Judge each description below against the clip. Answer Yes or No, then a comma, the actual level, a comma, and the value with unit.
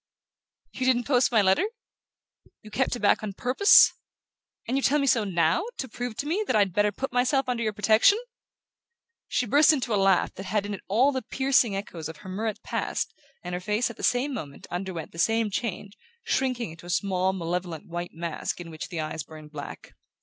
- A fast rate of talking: Yes, fast, 210 wpm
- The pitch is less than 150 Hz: No, high, 210 Hz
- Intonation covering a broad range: Yes, wide, 5.9 semitones